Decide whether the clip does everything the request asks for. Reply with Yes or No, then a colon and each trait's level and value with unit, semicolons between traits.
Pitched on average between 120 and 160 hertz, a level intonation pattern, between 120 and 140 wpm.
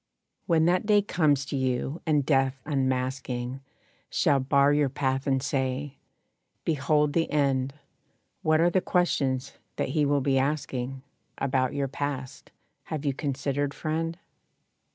Yes: medium, 140 Hz; narrow, 2.3 semitones; slow, 135 wpm